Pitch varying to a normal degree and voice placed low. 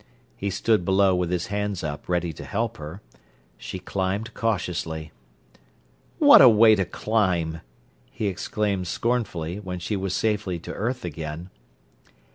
Yes: average, 3.4 semitones; very low, 95 Hz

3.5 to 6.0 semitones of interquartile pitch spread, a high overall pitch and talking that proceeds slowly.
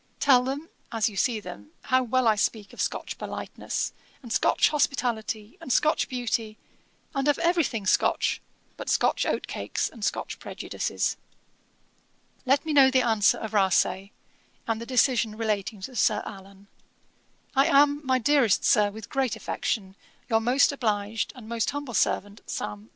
No: average, 4.1 semitones; high, 230 Hz; average, 160 wpm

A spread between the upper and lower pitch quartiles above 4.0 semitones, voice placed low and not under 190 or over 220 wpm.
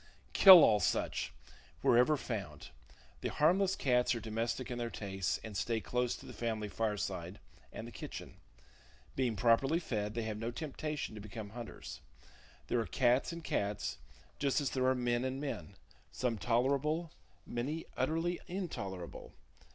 No: average, 4.5 semitones; low, 120 Hz; average, 150 wpm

